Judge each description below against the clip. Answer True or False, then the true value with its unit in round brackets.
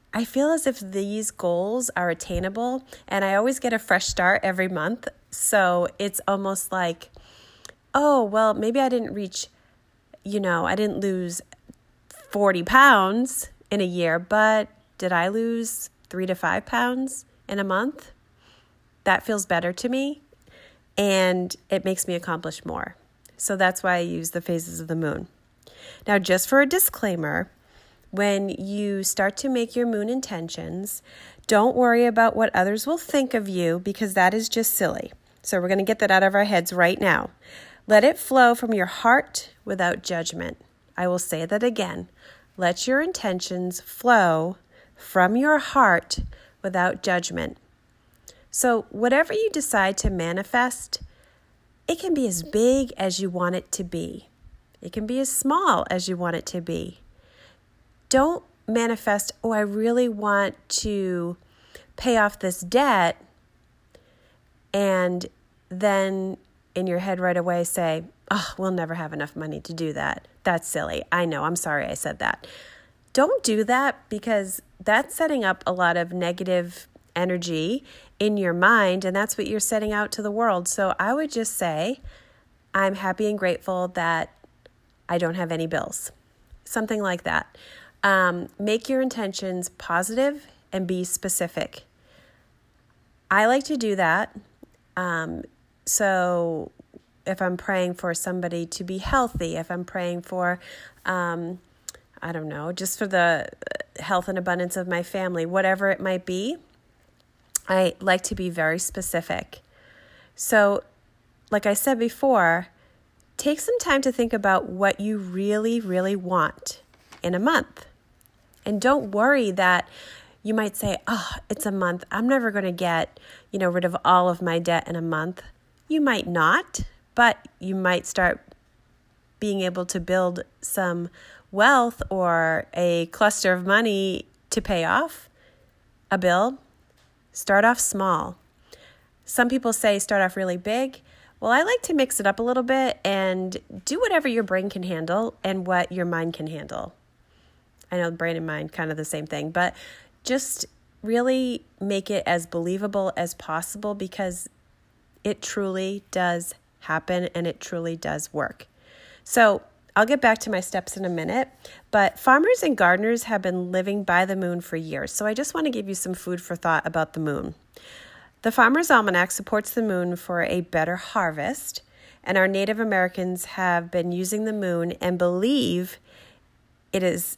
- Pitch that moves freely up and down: False (4.1 semitones)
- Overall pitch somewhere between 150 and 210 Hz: True (190 Hz)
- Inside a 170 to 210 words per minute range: False (160 wpm)